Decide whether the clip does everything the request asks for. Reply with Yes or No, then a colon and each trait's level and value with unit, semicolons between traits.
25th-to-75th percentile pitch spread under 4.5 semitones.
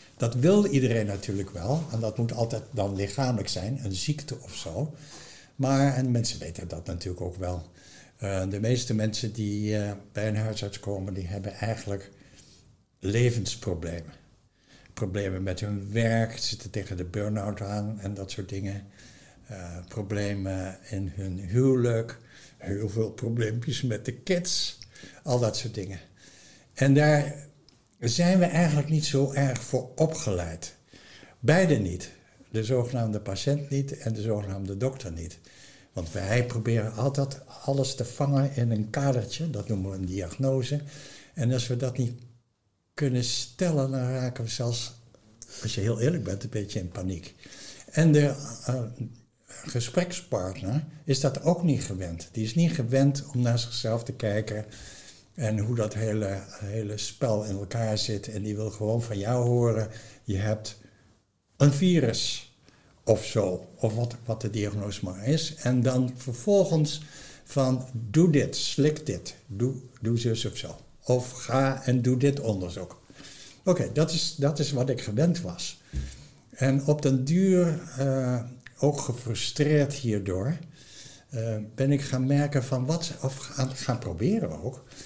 No: average, 4.9 semitones